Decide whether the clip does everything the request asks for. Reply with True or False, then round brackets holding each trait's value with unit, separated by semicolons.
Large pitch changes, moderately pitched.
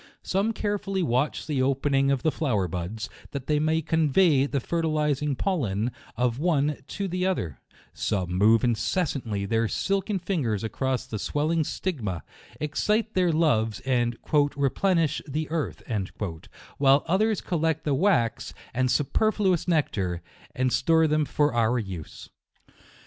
True (5.9 semitones; 145 Hz)